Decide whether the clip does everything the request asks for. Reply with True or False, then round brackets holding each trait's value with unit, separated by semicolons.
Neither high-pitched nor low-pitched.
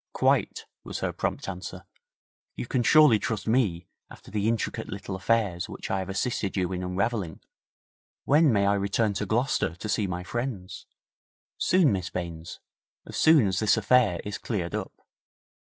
False (100 Hz)